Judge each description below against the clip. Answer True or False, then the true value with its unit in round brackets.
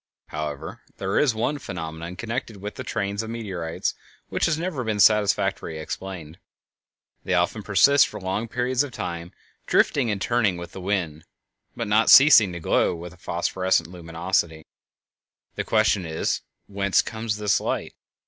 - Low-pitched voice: True (100 Hz)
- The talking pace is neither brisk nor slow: True (155 wpm)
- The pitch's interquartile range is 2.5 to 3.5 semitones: False (4.5 semitones)